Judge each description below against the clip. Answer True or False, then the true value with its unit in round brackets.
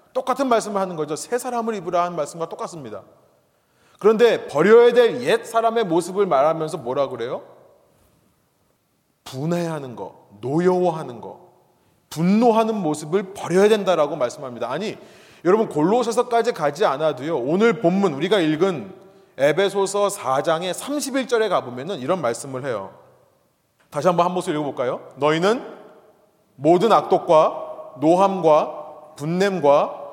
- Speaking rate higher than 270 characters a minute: True (295 characters per minute)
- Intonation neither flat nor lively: False (6.1 semitones)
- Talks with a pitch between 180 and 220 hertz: True (190 Hz)